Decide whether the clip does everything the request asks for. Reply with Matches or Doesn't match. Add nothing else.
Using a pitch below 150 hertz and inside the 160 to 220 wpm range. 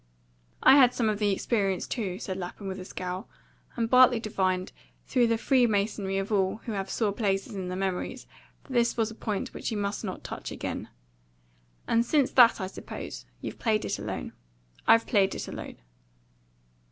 Doesn't match